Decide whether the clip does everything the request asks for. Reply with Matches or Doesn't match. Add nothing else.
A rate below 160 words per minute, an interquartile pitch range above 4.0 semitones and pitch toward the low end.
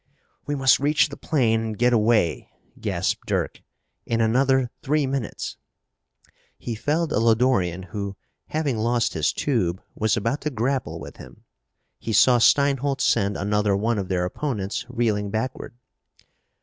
Matches